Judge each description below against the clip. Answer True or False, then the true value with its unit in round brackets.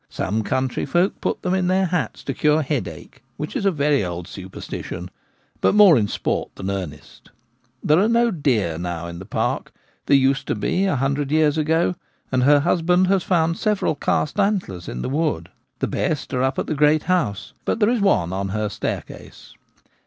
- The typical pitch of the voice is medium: True (145 Hz)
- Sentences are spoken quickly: False (195 wpm)